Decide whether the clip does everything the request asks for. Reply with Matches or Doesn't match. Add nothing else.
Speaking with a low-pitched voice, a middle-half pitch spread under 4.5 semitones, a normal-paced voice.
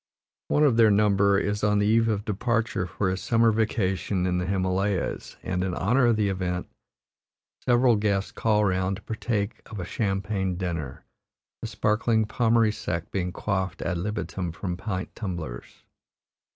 Matches